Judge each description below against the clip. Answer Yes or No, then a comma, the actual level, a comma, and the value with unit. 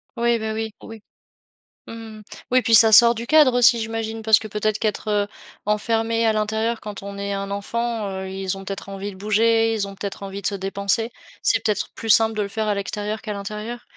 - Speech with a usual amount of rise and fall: No, narrow, 2.1 semitones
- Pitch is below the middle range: No, high, 215 Hz